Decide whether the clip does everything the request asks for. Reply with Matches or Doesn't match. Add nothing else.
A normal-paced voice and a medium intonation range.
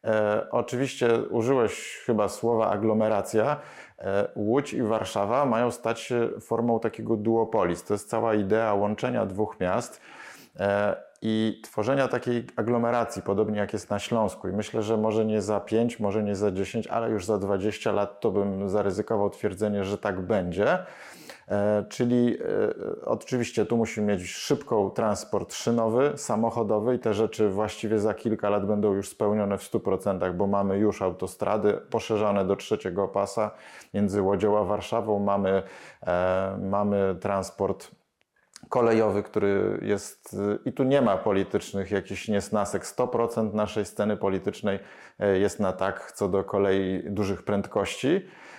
Doesn't match